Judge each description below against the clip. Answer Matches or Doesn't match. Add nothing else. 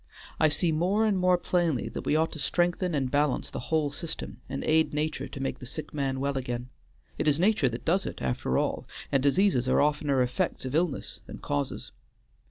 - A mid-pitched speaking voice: Matches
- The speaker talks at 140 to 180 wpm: Doesn't match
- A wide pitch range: Doesn't match